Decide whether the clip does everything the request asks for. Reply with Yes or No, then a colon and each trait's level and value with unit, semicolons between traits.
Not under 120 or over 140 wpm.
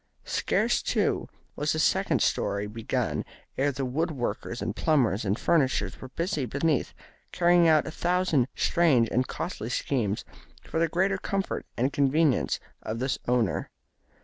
No: average, 150 wpm